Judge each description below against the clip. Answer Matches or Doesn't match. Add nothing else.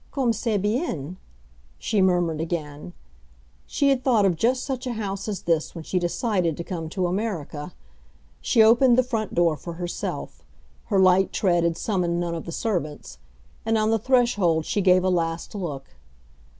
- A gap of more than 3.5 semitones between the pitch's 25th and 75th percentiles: Matches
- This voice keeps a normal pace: Matches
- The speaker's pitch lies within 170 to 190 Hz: Matches